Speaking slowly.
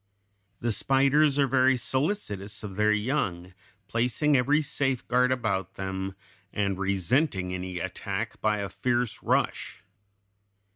Yes: slow, 115 wpm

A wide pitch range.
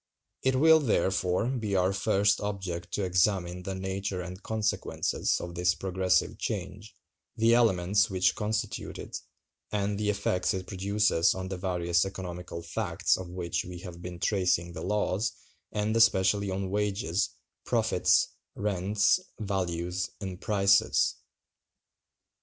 No: narrow, 2.4 semitones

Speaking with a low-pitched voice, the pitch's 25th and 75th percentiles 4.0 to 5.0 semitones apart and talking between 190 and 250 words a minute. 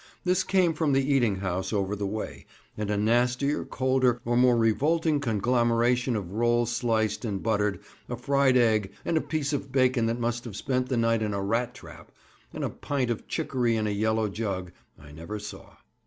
No: low, 120 Hz; average, 3.5 semitones; average, 195 wpm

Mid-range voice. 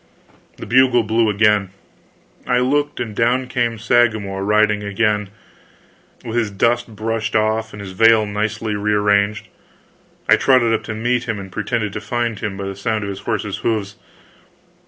No: low, 110 Hz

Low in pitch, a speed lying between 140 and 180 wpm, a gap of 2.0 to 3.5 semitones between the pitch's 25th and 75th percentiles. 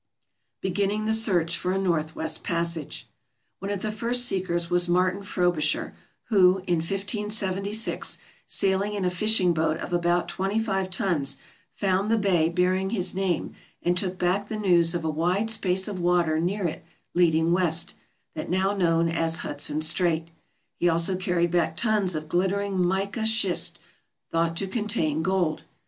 No: medium, 180 Hz; average, 155 wpm; average, 2.8 semitones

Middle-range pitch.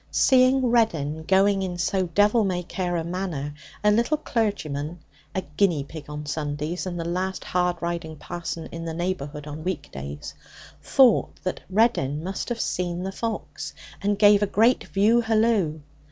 Yes: medium, 180 Hz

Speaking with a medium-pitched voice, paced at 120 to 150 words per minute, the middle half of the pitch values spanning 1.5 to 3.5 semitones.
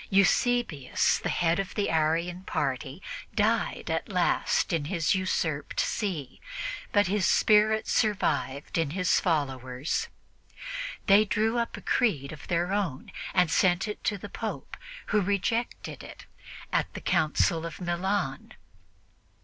No: medium, 180 Hz; slow, 135 wpm; average, 4.8 semitones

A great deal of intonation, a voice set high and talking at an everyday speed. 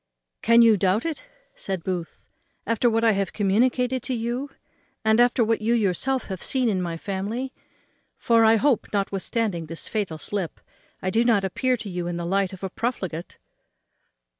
No: average, 3.9 semitones; high, 215 Hz; average, 175 wpm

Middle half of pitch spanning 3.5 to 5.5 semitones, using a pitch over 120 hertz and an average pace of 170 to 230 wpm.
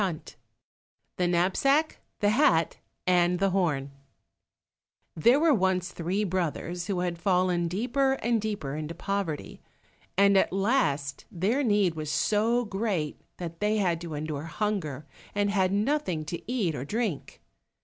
No: average, 4.1 semitones; medium, 185 Hz; average, 140 wpm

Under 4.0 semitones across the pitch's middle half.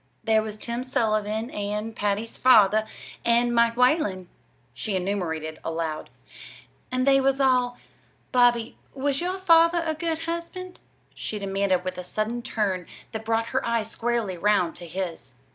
No: average, 4.4 semitones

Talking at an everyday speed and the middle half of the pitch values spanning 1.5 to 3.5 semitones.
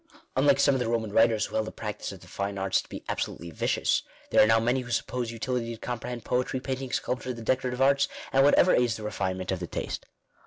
No: fast, 235 wpm; average, 3.0 semitones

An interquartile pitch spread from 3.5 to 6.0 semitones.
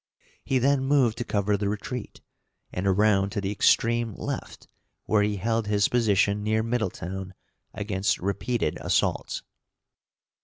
No: average, 2.7 semitones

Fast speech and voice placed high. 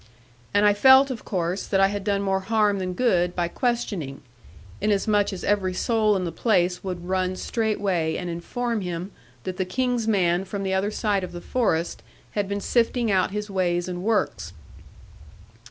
No: average, 180 wpm; high, 195 Hz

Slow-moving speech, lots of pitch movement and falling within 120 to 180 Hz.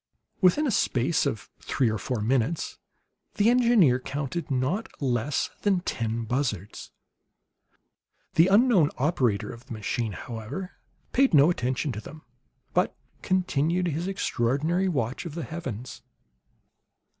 Yes: slow, 125 wpm; wide, 6.8 semitones; medium, 140 Hz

